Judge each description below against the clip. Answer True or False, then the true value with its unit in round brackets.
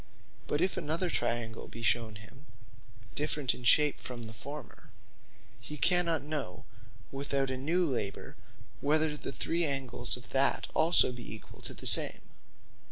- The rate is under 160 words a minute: True (150 wpm)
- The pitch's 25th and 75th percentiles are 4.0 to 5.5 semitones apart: True (4.4 semitones)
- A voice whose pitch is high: False (140 Hz)